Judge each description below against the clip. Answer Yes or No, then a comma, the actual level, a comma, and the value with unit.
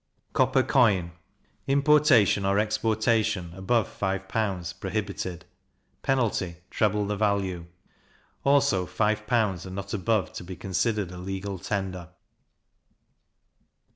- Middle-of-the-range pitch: No, low, 100 Hz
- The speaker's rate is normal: No, slow, 110 wpm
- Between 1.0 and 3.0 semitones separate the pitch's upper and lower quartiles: Yes, average, 2.7 semitones